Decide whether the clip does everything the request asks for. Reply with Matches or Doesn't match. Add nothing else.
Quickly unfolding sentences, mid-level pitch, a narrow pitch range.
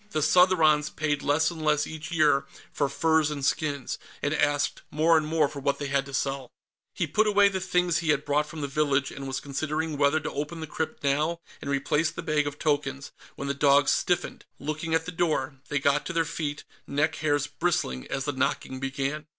Matches